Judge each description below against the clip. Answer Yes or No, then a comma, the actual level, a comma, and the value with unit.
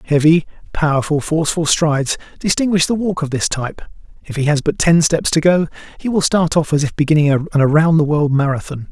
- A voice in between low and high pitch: Yes, medium, 155 Hz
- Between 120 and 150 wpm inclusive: No, average, 200 wpm